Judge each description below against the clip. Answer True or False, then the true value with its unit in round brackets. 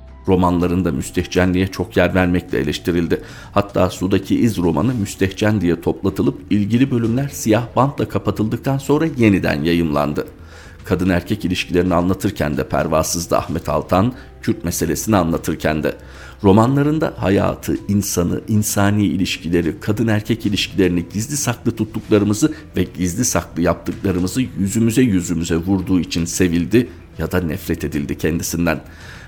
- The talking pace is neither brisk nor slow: True (120 wpm)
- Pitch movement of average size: True (3.9 semitones)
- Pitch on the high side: False (95 Hz)